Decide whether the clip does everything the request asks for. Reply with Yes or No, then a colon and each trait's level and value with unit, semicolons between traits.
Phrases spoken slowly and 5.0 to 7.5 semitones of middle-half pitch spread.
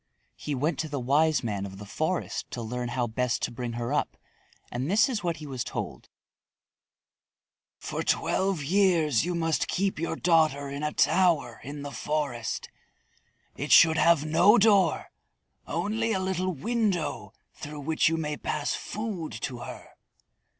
No: average, 160 wpm; wide, 5.5 semitones